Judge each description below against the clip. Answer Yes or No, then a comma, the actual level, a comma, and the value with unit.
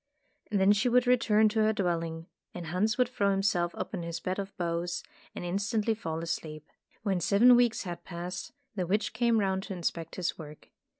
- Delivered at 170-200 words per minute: Yes, average, 185 wpm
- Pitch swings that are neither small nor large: Yes, average, 4.0 semitones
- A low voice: No, high, 190 Hz